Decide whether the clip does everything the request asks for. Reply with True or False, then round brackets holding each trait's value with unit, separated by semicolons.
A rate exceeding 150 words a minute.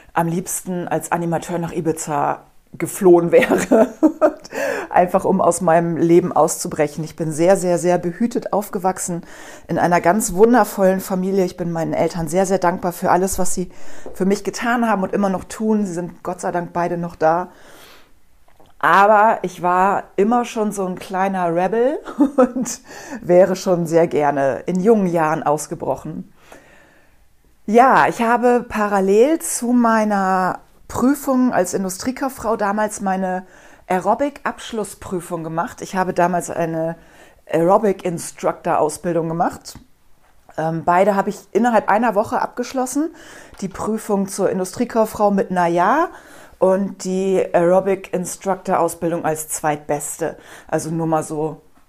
False (130 wpm)